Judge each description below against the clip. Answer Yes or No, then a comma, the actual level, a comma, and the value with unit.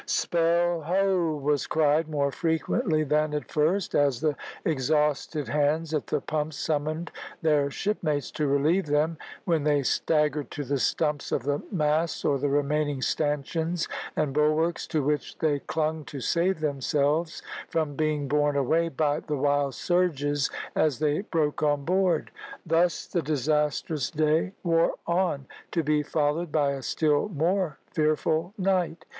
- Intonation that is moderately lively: No, narrow, 2.2 semitones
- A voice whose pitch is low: No, medium, 155 Hz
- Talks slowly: No, average, 150 wpm